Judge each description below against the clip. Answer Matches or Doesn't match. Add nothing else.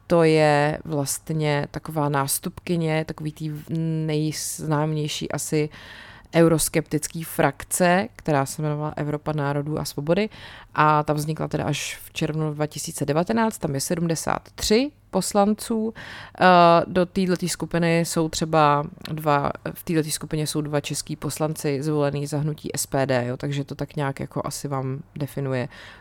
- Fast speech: Doesn't match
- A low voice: Doesn't match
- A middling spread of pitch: Doesn't match